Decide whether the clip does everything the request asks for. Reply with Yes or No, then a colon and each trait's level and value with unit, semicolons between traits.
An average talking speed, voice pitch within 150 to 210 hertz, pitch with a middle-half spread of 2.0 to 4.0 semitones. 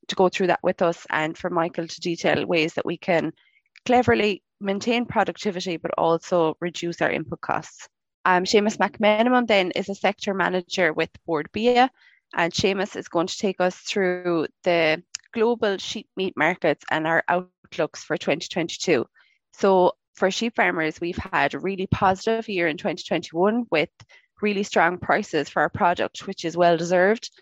Yes: average, 165 wpm; medium, 185 Hz; average, 3.5 semitones